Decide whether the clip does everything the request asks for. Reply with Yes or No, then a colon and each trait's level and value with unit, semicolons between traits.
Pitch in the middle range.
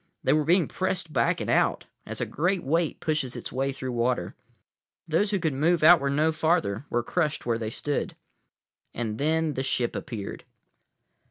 Yes: medium, 150 Hz